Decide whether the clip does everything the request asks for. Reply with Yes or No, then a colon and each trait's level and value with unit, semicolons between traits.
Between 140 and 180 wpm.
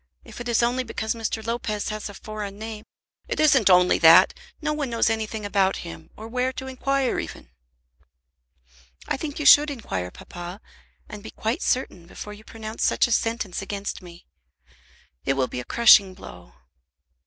Yes: average, 175 wpm